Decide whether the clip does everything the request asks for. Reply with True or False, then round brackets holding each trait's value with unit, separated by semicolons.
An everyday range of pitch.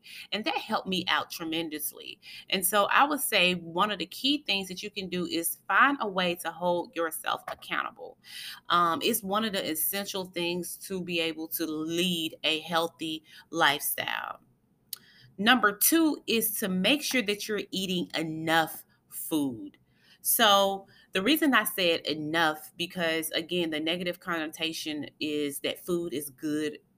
True (4.0 semitones)